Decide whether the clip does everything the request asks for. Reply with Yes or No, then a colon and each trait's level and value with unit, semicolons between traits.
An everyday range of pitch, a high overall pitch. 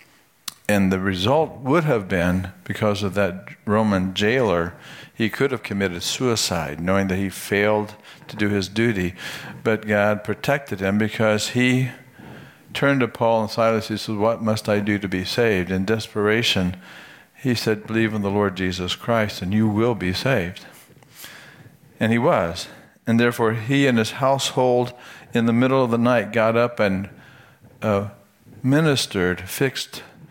No: average, 3.4 semitones; low, 110 Hz